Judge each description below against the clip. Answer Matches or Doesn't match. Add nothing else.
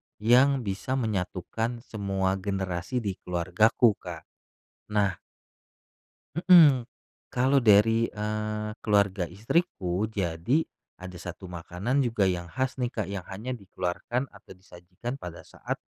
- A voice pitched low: Matches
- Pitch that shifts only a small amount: Doesn't match